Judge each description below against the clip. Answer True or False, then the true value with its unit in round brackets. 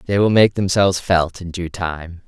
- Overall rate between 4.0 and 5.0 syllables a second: True (4.5 syllables/s)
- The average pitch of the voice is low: True (90 Hz)